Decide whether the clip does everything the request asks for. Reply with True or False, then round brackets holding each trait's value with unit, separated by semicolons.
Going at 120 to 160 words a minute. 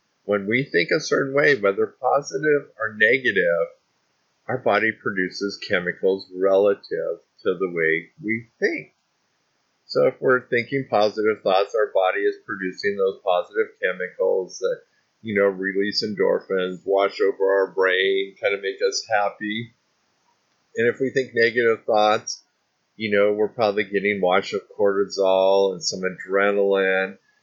True (140 wpm)